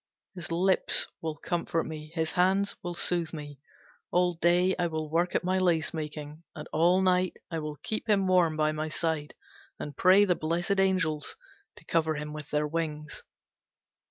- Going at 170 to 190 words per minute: Yes, average, 175 wpm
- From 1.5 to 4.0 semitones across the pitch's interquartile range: Yes, average, 2.8 semitones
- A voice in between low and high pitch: Yes, medium, 165 Hz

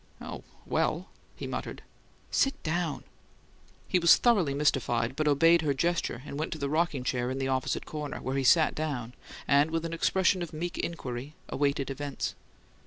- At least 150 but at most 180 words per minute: Yes, average, 175 wpm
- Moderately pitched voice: Yes, medium, 150 Hz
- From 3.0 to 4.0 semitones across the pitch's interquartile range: Yes, average, 3.7 semitones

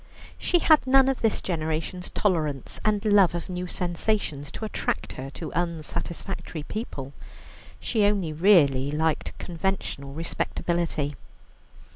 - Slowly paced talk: Yes, slow, 120 wpm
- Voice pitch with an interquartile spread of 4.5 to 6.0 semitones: Yes, average, 4.8 semitones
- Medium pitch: Yes, medium, 175 Hz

